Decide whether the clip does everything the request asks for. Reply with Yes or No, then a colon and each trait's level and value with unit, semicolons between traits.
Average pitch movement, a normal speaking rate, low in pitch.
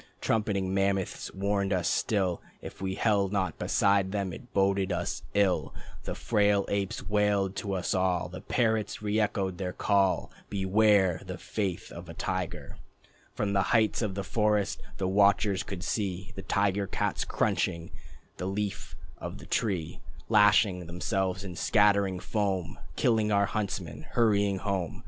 No: narrow, 1.6 semitones; average, 150 wpm; low, 100 Hz